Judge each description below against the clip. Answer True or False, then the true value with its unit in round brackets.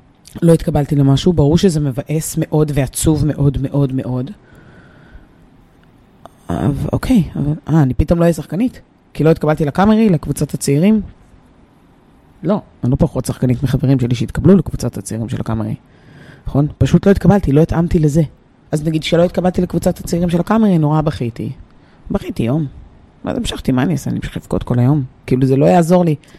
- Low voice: False (150 Hz)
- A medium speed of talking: False (160 wpm)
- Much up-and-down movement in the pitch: False (4.5 semitones)